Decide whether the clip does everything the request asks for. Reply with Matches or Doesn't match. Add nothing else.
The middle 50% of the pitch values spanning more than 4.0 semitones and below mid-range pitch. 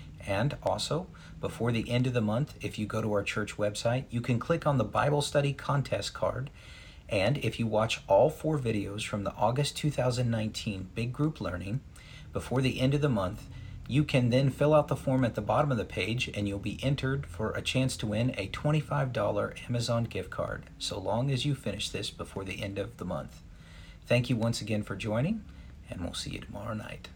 Matches